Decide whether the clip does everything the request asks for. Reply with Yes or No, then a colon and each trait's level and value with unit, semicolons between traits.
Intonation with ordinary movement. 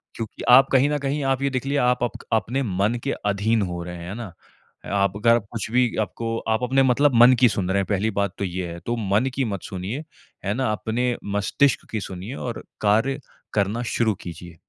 Yes: average, 4.2 semitones